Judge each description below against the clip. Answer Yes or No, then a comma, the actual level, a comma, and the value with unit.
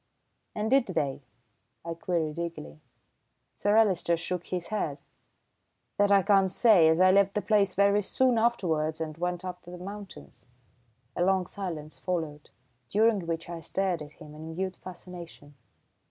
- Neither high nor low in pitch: Yes, medium, 180 Hz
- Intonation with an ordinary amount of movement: Yes, average, 3.5 semitones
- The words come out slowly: No, average, 155 wpm